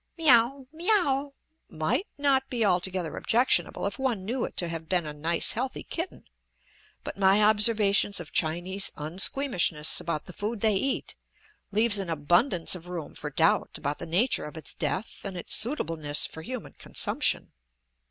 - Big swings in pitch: Yes, wide, 6.7 semitones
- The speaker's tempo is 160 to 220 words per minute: Yes, average, 165 wpm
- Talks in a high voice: Yes, high, 195 Hz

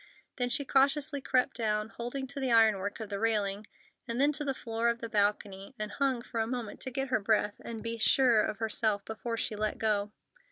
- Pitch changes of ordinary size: Yes, average, 3.4 semitones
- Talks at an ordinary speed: No, fast, 215 wpm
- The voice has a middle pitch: No, high, 230 Hz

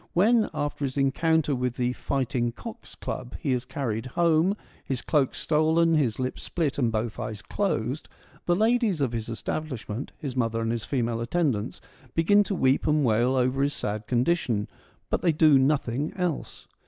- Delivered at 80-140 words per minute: No, average, 180 wpm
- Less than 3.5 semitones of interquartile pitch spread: No, average, 5.1 semitones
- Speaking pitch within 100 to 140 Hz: Yes, low, 135 Hz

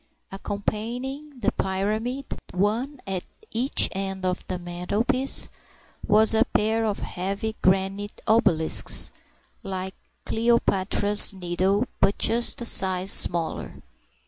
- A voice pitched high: Yes, high, 205 Hz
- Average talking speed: No, slow, 95 wpm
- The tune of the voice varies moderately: Yes, average, 3.3 semitones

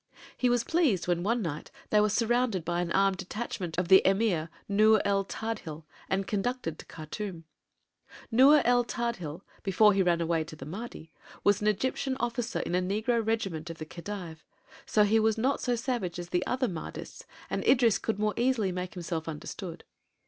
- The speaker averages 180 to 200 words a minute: Yes, average, 185 wpm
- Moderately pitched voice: No, high, 200 Hz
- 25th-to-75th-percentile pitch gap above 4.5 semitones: Yes, average, 4.9 semitones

